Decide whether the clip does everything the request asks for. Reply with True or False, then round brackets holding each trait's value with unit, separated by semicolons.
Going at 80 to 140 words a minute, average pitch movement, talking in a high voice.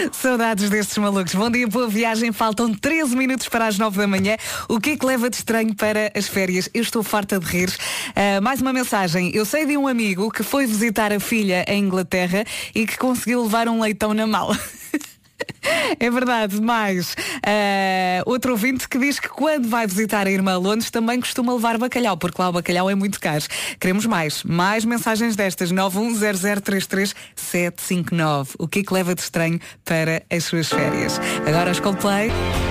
False (185 wpm; 3.8 semitones; 210 Hz)